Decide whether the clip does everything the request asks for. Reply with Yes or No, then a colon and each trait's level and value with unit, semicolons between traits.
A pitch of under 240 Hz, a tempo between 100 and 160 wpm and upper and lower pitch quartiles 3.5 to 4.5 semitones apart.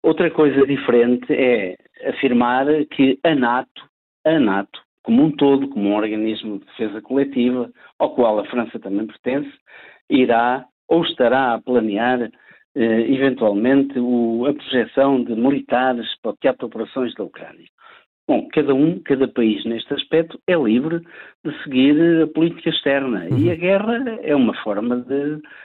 Yes: low, 135 Hz; average, 155 wpm; average, 3.9 semitones